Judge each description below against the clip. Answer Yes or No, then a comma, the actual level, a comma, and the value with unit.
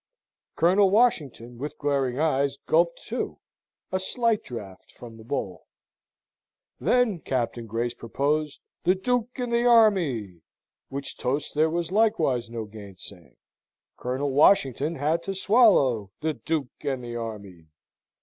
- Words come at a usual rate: No, slow, 130 wpm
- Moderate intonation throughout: No, wide, 8.1 semitones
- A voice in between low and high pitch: Yes, medium, 145 Hz